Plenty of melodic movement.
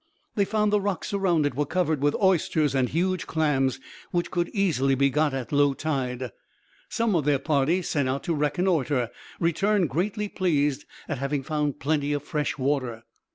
No: average, 4.4 semitones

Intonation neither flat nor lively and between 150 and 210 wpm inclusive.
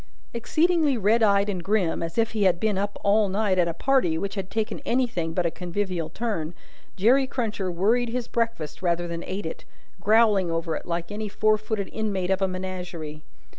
Yes: average, 4.1 semitones; average, 195 wpm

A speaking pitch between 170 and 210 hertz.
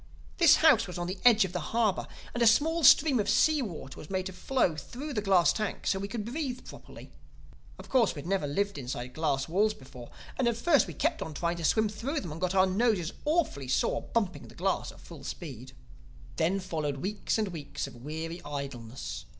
Yes: high, 190 Hz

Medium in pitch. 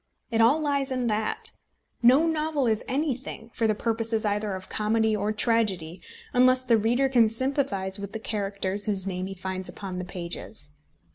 No: high, 220 Hz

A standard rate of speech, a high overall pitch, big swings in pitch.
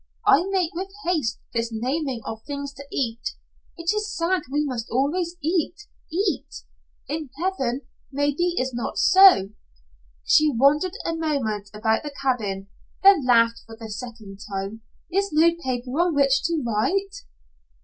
Yes: average, 150 wpm; very high, 280 Hz; wide, 6.6 semitones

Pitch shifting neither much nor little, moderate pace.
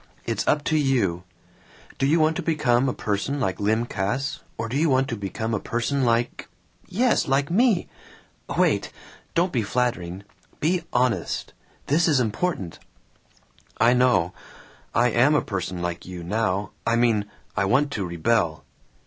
No: wide, 6.0 semitones; average, 155 wpm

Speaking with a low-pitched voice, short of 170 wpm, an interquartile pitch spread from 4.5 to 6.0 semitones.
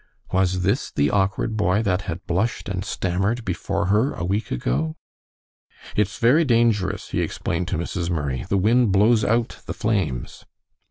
No: very low, 95 Hz; average, 160 wpm; average, 3.9 semitones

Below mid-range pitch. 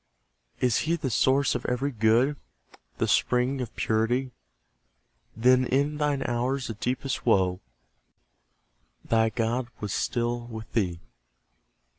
Yes: low, 125 Hz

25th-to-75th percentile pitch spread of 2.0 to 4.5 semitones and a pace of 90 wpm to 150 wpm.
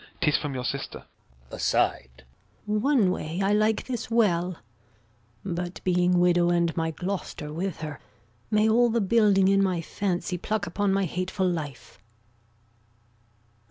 Yes: average, 3.4 semitones; average, 140 wpm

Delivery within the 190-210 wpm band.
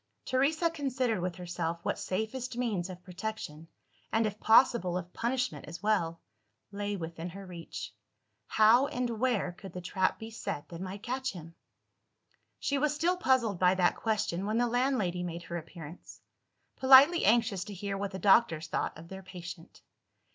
No: average, 165 wpm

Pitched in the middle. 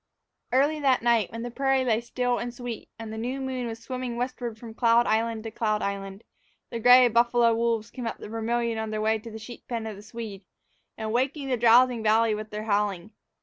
No: high, 230 Hz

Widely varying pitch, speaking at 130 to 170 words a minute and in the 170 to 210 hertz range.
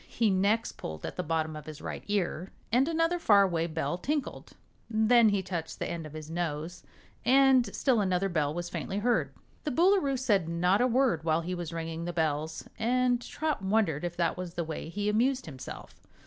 No: wide, 6.7 semitones; average, 200 wpm; medium, 185 Hz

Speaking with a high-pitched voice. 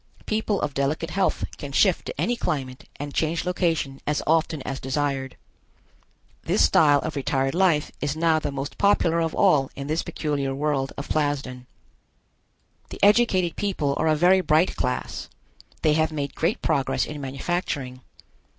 No: medium, 150 Hz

